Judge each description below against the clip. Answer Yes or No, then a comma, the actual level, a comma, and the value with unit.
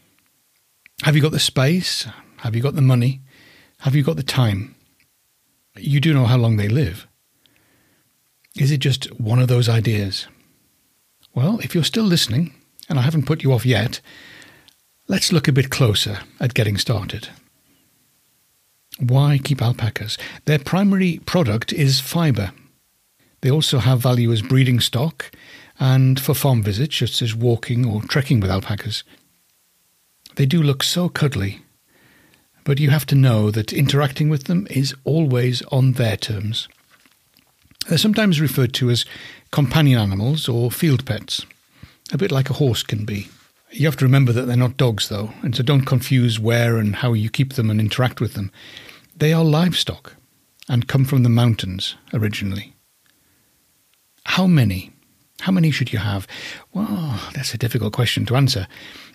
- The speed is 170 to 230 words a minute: No, average, 160 wpm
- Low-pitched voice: Yes, low, 130 Hz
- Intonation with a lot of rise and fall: No, average, 4.2 semitones